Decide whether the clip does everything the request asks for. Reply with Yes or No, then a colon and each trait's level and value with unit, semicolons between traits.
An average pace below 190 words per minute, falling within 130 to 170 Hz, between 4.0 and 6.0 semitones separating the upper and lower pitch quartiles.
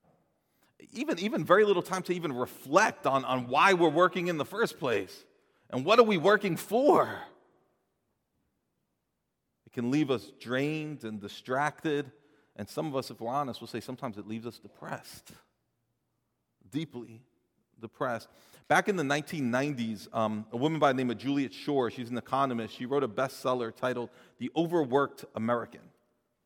Yes: average, 160 wpm; low, 135 Hz; average, 4.7 semitones